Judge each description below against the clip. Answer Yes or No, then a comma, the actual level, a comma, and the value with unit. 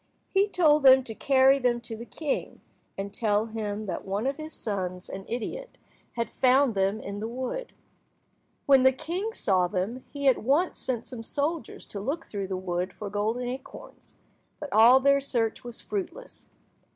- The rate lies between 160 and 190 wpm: Yes, average, 175 wpm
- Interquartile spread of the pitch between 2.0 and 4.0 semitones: No, average, 5.2 semitones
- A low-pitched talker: No, high, 240 Hz